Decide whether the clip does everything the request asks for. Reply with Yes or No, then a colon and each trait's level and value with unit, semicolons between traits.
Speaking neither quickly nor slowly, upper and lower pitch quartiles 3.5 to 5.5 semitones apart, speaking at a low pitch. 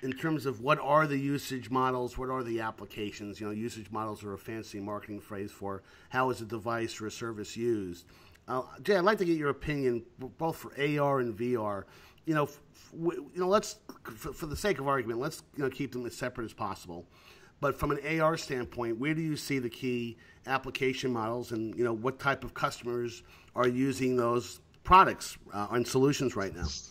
No: fast, 210 wpm; average, 4.2 semitones; low, 120 Hz